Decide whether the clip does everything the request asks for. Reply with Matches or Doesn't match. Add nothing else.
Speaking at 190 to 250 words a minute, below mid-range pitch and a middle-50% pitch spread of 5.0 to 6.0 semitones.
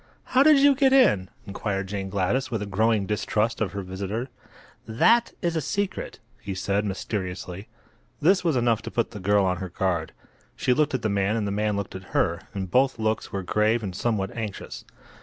Doesn't match